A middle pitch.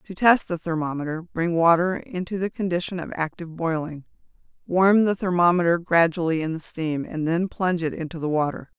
Yes: medium, 170 Hz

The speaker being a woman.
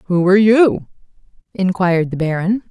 Yes: female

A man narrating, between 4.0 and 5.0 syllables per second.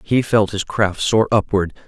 Yes: male; 4.3 syllables/s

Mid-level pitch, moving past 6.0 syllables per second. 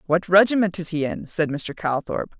No: medium, 170 Hz; 5.0 syllables/s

